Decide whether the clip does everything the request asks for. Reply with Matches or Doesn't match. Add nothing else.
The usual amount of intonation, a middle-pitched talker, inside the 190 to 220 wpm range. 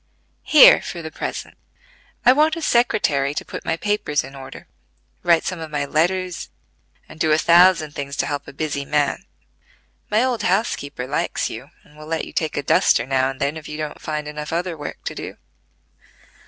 Matches